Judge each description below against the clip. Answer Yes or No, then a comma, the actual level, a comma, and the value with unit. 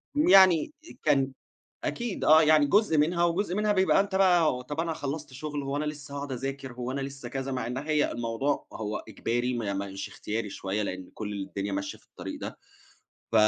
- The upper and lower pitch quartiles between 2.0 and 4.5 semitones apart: No, average, 5.2 semitones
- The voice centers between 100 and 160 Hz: Yes, medium, 140 Hz